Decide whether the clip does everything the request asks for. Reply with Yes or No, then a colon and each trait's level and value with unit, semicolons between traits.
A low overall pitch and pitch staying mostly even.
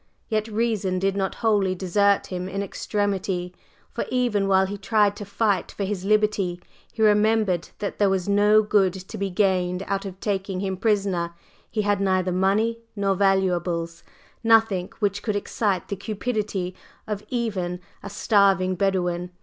No: high, 195 Hz; narrow, 2.0 semitones